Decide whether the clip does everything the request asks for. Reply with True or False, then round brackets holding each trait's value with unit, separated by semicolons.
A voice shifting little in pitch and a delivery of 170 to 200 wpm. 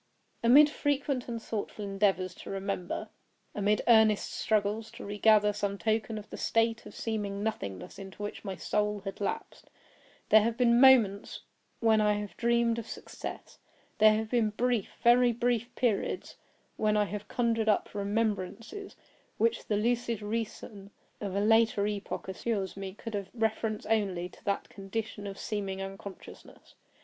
False (2.3 semitones; 155 wpm)